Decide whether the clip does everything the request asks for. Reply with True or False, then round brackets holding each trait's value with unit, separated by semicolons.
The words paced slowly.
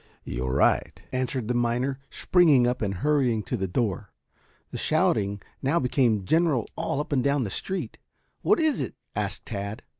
False (170 wpm)